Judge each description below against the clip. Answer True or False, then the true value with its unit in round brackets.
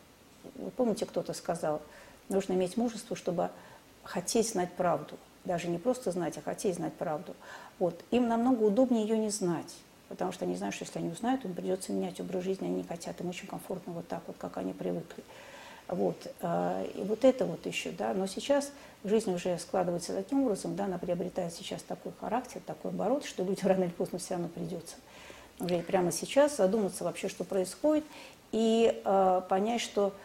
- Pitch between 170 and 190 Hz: True (185 Hz)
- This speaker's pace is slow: False (180 wpm)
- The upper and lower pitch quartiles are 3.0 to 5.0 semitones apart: True (4.2 semitones)